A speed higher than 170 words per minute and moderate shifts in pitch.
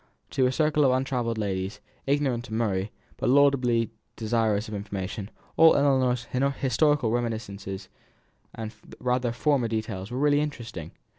No: slow, 135 wpm; average, 3.8 semitones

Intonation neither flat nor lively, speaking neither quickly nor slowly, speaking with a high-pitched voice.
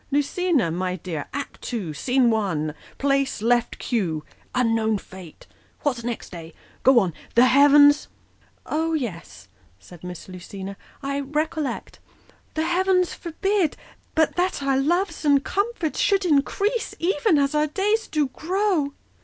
No: wide, 7.7 semitones; average, 160 wpm; very high, 275 Hz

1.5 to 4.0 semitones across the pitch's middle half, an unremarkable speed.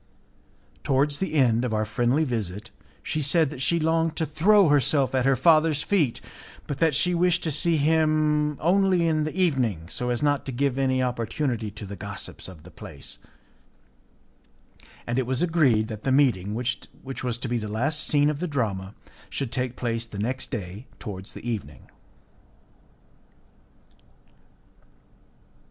No: average, 5.1 semitones; average, 160 wpm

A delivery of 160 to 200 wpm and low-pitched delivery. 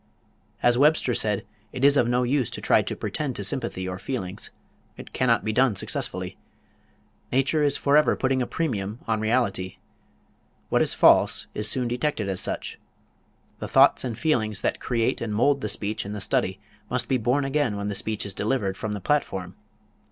Yes: average, 185 wpm; low, 115 Hz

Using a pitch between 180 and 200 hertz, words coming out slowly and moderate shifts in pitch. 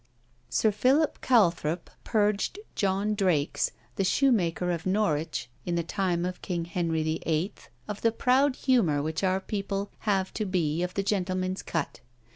No: medium, 185 Hz; average, 150 wpm; average, 3.6 semitones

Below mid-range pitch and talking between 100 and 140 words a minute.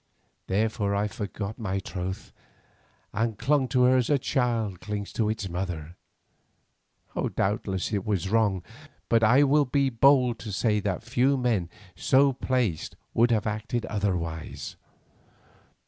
Yes: low, 110 Hz; slow, 135 wpm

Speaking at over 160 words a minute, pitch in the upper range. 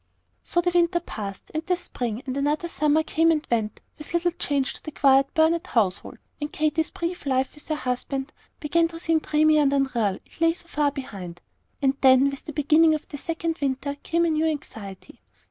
Yes: average, 200 wpm; very high, 300 Hz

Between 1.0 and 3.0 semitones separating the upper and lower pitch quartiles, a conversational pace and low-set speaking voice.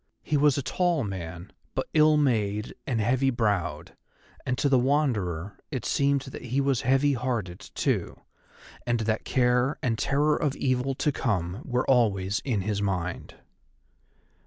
No: average, 5.0 semitones; average, 155 wpm; low, 125 Hz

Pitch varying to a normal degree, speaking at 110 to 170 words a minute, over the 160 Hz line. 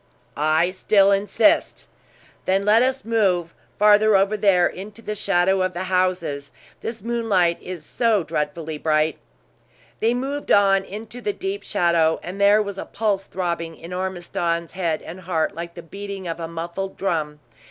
Yes: average, 3.5 semitones; average, 160 wpm; high, 190 Hz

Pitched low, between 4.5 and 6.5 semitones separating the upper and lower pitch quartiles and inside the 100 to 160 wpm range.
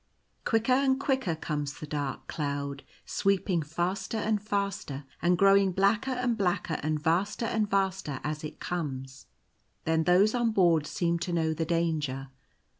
No: medium, 175 Hz; average, 4.9 semitones; average, 150 wpm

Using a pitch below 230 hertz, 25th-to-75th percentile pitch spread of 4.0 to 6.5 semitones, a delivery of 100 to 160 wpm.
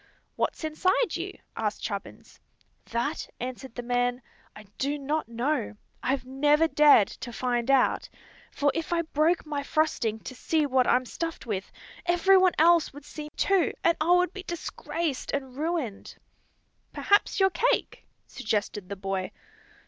No: very high, 290 Hz; average, 5.1 semitones; average, 150 wpm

